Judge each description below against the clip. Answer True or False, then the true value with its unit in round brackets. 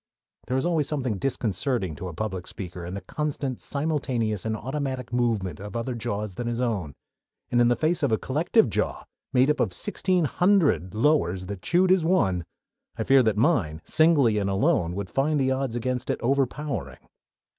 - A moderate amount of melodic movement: False (6.3 semitones)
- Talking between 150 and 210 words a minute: True (185 wpm)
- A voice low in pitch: True (120 Hz)